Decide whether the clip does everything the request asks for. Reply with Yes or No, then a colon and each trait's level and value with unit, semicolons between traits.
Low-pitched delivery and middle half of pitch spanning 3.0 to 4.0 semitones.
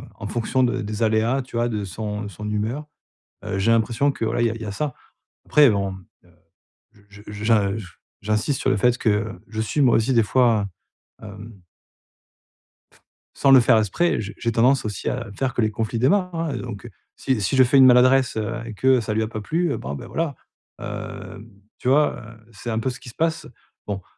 Yes: low, 115 Hz; average, 3.6 semitones